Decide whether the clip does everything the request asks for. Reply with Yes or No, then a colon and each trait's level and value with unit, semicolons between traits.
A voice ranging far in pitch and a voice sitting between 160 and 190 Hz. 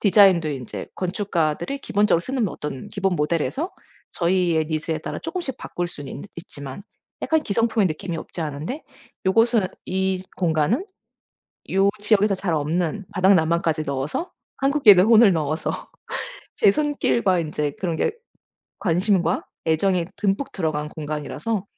No: average, 4.7 semitones; medium, 185 Hz